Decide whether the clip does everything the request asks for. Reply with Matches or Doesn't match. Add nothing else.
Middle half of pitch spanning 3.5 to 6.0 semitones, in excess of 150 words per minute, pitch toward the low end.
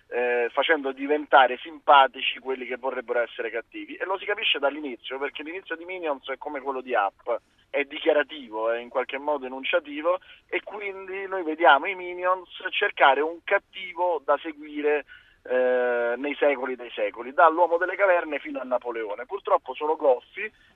Doesn't match